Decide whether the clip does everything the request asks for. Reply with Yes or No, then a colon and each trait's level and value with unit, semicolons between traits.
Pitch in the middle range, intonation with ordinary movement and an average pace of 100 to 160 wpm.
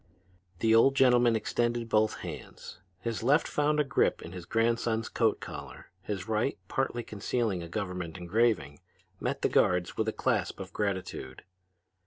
No: low, 110 Hz; average, 4.3 semitones; average, 155 wpm